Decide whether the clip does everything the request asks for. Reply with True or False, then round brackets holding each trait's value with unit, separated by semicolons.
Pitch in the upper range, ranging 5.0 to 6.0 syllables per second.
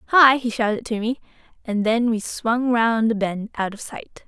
False (230 Hz; 4.6 syllables/s)